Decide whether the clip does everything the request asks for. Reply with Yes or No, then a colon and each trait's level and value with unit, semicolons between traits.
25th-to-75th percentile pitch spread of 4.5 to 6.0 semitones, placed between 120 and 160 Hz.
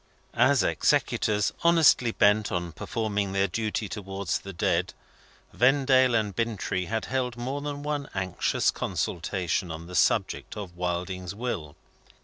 No: average, 5.1 semitones; low, 105 Hz